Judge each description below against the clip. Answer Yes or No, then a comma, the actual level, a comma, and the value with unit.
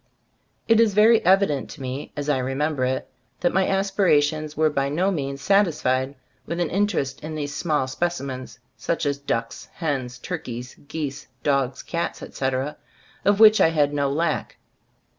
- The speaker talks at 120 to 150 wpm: No, average, 160 wpm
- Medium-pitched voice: Yes, medium, 150 Hz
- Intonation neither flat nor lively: Yes, average, 4.3 semitones